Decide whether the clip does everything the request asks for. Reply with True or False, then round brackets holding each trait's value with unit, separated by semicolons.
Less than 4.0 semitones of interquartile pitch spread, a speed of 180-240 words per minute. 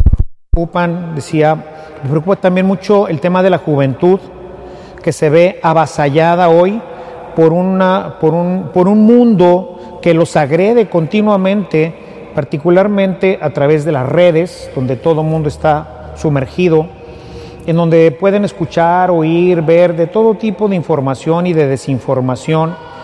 False (2.8 semitones; 135 wpm)